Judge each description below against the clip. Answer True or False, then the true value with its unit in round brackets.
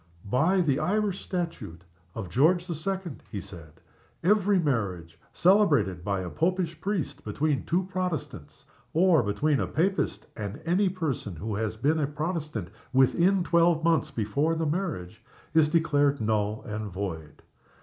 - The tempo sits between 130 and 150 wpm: True (145 wpm)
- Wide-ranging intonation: True (8.7 semitones)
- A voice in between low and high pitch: True (150 Hz)